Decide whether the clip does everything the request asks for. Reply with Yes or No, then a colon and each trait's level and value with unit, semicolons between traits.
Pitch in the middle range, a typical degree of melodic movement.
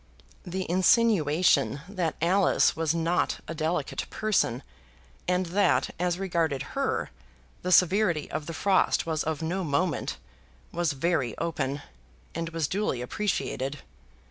Yes: medium, 170 Hz; average, 3.2 semitones